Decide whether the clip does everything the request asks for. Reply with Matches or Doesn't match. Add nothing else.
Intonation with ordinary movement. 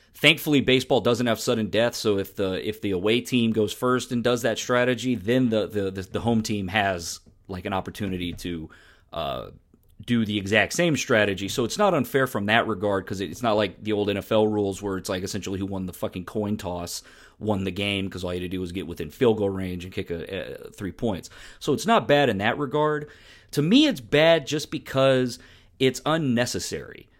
Matches